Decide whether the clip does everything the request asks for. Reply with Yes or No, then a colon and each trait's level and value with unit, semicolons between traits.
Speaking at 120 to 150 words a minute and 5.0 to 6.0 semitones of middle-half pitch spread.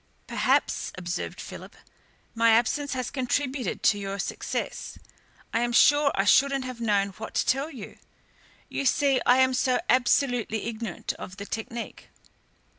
No: average, 145 wpm; average, 3.2 semitones